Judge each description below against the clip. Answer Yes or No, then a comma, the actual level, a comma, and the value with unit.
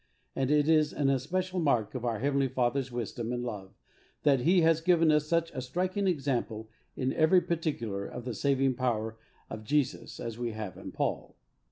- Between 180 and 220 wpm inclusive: Yes, average, 185 wpm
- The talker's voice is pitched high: No, low, 135 Hz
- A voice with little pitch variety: No, average, 4.9 semitones